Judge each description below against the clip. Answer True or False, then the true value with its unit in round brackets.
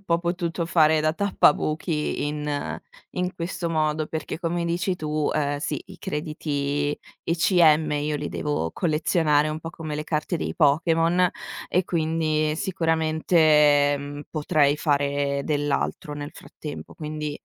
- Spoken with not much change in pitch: True (2.1 semitones)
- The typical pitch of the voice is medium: True (155 Hz)